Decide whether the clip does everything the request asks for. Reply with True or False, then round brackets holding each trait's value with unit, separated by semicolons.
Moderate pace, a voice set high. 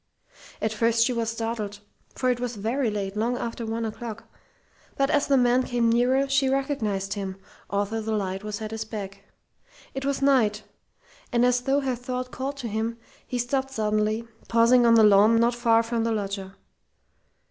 True (180 wpm; 230 Hz)